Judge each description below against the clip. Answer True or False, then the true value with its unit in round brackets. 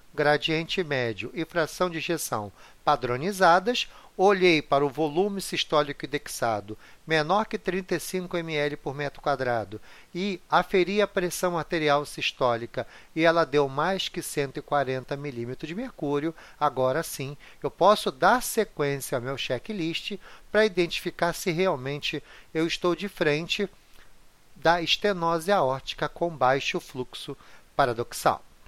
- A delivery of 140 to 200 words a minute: False (125 wpm)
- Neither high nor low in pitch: True (160 Hz)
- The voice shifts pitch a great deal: False (4.2 semitones)